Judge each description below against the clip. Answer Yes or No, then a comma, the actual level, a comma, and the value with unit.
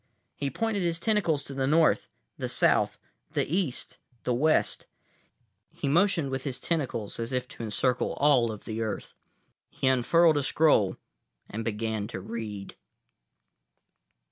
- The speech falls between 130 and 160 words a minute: Yes, average, 140 wpm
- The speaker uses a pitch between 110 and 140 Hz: Yes, low, 135 Hz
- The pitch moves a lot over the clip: Yes, wide, 5.9 semitones